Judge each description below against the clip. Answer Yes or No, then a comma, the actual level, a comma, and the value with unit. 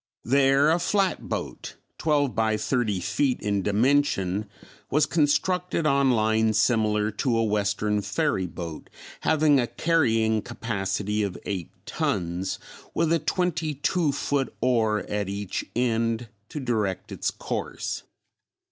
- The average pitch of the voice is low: Yes, low, 115 Hz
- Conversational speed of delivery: No, slow, 125 wpm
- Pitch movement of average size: No, wide, 5.7 semitones